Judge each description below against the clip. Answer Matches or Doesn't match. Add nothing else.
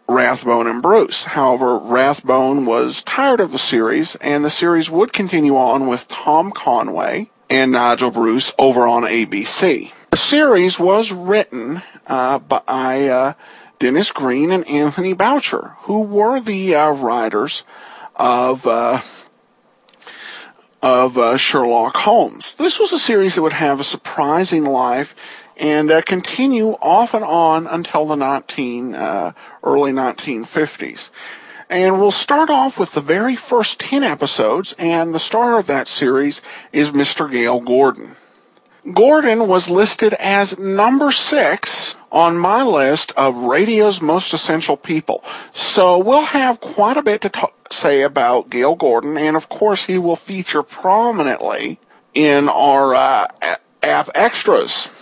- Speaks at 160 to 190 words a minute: Doesn't match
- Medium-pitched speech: Matches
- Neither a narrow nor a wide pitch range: Doesn't match